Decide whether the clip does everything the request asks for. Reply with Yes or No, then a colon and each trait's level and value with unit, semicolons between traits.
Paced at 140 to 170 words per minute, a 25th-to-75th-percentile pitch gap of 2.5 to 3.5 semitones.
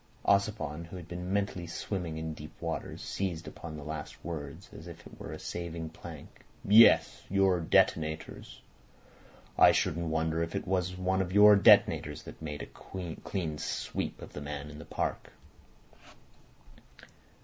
Yes: average, 155 wpm; average, 2.9 semitones